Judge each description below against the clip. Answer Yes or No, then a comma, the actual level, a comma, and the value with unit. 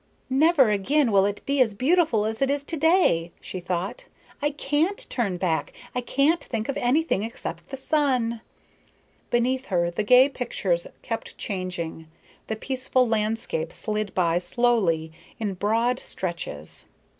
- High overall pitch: Yes, high, 230 Hz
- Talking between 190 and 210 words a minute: No, average, 145 wpm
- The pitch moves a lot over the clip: Yes, wide, 6.2 semitones